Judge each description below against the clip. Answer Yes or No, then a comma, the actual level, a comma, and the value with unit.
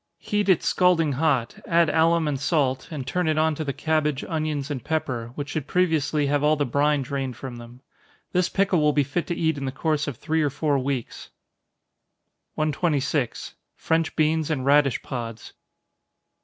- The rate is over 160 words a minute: Yes, average, 180 wpm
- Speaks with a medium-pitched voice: Yes, medium, 150 Hz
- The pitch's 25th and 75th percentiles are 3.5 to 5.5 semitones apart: No, narrow, 2.6 semitones